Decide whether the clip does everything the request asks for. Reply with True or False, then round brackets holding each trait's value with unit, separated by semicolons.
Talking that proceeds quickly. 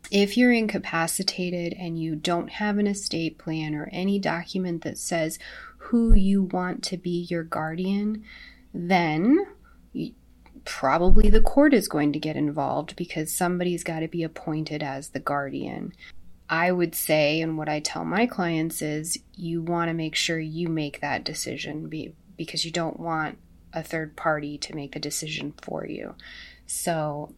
False (165 wpm)